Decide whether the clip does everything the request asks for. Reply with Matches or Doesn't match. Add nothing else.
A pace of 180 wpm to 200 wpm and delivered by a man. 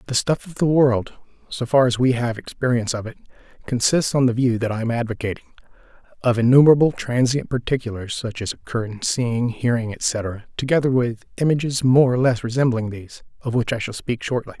Matches